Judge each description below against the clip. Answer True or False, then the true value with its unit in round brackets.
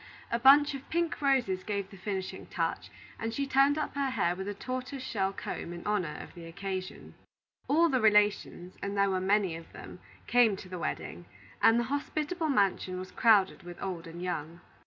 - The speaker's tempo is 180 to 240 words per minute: True (195 wpm)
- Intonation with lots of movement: True (6.0 semitones)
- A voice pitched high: True (205 Hz)